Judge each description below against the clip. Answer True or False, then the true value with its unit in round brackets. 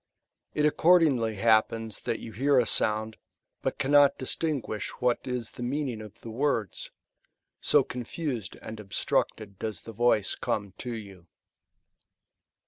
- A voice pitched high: False (115 Hz)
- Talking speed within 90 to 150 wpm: True (135 wpm)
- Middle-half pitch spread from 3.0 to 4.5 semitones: True (3.7 semitones)